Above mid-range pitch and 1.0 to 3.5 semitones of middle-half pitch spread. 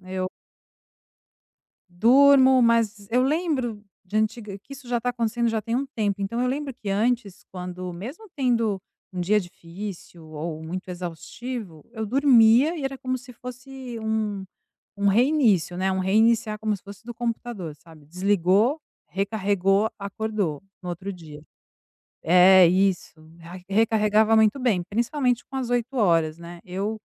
No: high, 215 Hz; average, 4.7 semitones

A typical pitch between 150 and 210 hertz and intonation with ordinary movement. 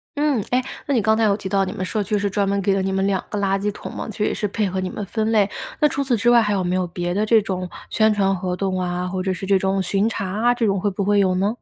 No: high, 200 Hz; narrow, 2.3 semitones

